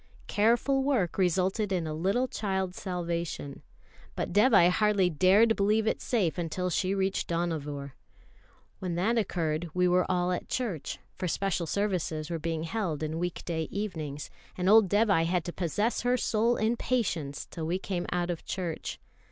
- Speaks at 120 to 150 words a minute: No, average, 165 wpm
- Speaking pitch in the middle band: Yes, medium, 180 Hz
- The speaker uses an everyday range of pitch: Yes, average, 3.9 semitones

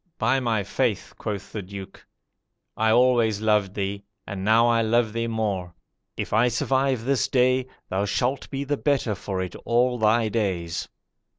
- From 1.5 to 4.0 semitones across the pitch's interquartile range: Yes, average, 3.5 semitones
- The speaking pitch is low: Yes, low, 110 Hz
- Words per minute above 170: No, average, 165 wpm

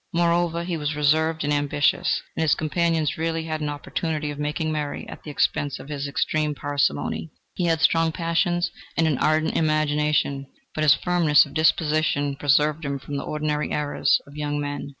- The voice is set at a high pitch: No, medium, 150 Hz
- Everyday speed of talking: Yes, average, 180 wpm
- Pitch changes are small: Yes, narrow, 1.8 semitones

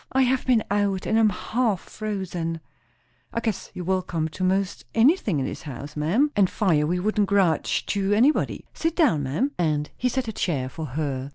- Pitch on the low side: No, high, 190 Hz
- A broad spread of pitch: Yes, wide, 6.0 semitones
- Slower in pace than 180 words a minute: No, average, 195 wpm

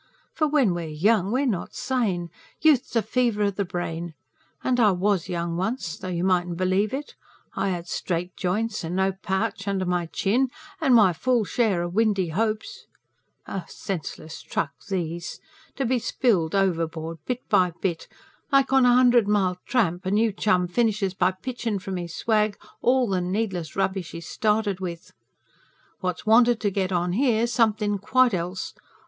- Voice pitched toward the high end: Yes, high, 195 Hz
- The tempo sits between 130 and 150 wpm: No, average, 165 wpm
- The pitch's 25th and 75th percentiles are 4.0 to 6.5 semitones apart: Yes, average, 4.3 semitones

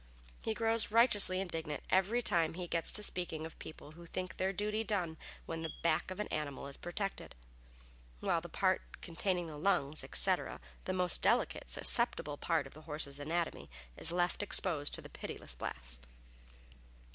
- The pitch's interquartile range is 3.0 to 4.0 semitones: Yes, average, 3.7 semitones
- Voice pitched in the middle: Yes, medium, 170 Hz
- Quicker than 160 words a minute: Yes, average, 170 wpm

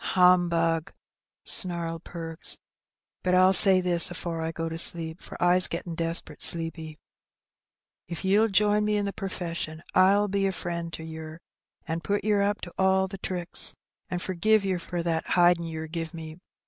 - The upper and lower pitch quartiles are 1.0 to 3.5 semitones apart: Yes, narrow, 2.5 semitones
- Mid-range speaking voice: Yes, medium, 175 Hz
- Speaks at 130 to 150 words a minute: No, average, 170 wpm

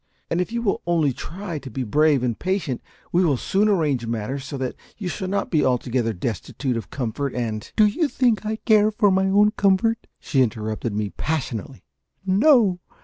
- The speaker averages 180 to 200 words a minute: Yes, average, 195 wpm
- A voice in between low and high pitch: Yes, medium, 155 Hz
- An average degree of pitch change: No, wide, 8.2 semitones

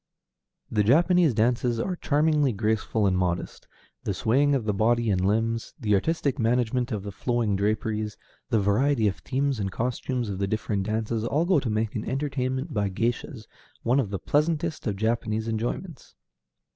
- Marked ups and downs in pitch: No, average, 4.1 semitones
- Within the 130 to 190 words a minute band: Yes, average, 170 wpm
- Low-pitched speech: Yes, low, 115 Hz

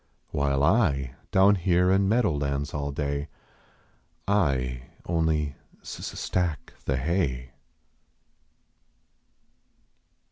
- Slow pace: Yes, slow, 95 wpm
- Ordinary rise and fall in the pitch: Yes, average, 4.8 semitones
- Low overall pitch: Yes, very low, 75 Hz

